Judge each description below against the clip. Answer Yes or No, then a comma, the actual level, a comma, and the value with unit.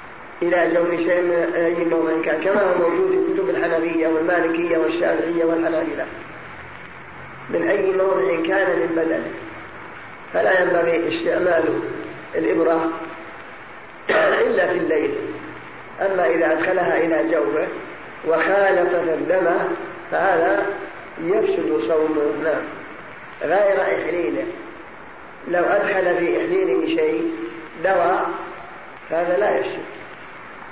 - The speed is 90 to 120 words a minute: Yes, average, 100 wpm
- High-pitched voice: No, medium, 170 Hz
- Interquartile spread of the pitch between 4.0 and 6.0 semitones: No, average, 2.7 semitones